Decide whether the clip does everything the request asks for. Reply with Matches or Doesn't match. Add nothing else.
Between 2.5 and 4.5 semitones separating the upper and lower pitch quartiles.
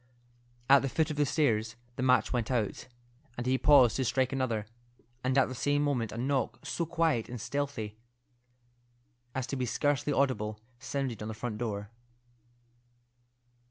Matches